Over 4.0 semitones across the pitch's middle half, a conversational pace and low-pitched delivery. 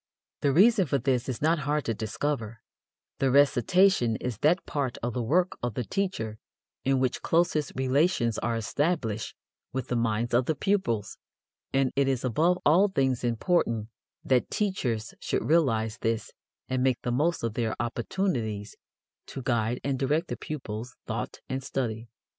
Yes: average, 4.6 semitones; average, 160 wpm; low, 130 Hz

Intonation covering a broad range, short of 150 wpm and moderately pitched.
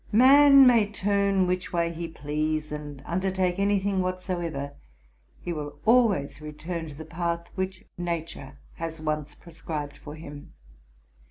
No: average, 3.9 semitones; average, 140 wpm; medium, 170 Hz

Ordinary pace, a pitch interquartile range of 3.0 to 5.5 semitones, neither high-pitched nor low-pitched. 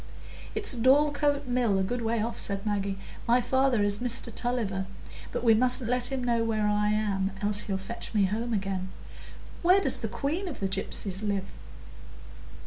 No: average, 175 wpm; average, 3.8 semitones; high, 225 Hz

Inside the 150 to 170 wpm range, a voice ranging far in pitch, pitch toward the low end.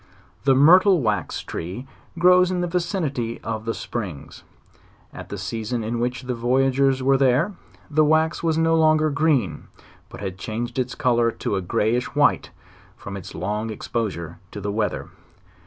Yes: average, 160 wpm; wide, 6.3 semitones; low, 125 Hz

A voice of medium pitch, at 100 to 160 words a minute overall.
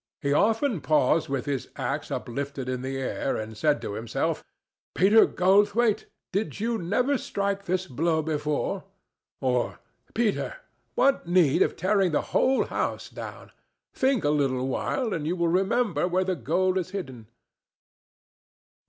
Yes: medium, 175 Hz; average, 145 wpm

